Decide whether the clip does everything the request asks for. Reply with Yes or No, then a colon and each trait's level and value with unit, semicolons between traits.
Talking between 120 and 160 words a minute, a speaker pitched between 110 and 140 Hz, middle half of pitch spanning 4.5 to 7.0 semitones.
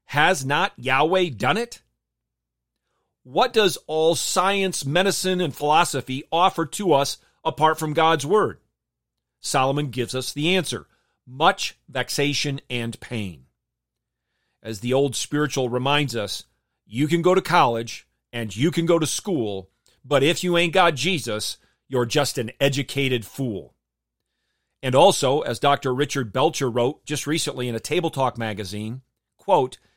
Yes: average, 140 wpm; low, 135 Hz; wide, 5.6 semitones